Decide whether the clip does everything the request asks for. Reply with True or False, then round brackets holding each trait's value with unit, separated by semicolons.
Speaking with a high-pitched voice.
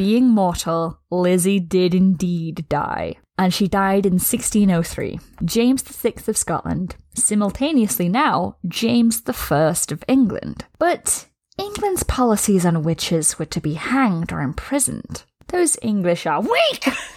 True (200 Hz)